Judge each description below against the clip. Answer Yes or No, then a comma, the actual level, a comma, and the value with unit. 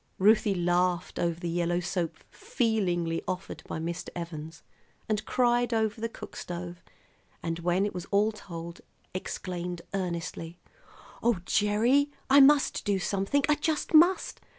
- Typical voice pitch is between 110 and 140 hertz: No, medium, 185 Hz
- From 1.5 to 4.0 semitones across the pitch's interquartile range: No, average, 4.4 semitones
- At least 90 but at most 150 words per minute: Yes, average, 140 wpm